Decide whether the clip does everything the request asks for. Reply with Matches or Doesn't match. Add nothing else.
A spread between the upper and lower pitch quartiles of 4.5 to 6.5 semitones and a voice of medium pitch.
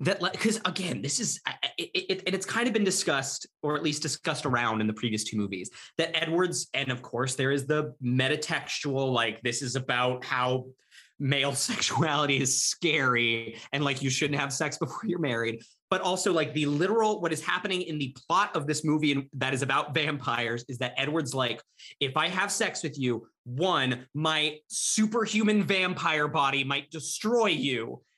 Matches